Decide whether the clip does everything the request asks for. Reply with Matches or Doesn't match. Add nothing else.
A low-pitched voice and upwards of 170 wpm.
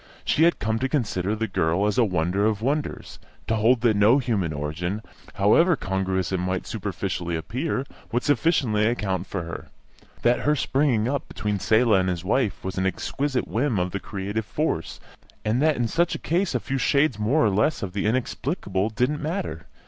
Matches